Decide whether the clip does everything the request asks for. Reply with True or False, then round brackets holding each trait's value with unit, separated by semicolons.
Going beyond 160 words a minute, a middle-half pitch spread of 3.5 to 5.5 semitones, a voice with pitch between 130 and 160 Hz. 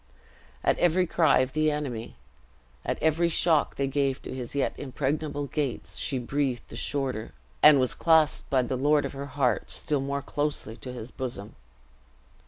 False (170 wpm; 2.6 semitones; 140 Hz)